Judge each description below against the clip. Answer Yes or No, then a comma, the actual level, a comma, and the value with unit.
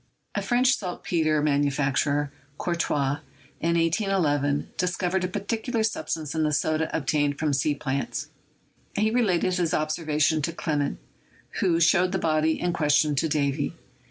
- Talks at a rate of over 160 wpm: No, average, 145 wpm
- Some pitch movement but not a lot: Yes, average, 3.6 semitones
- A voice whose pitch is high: No, medium, 160 Hz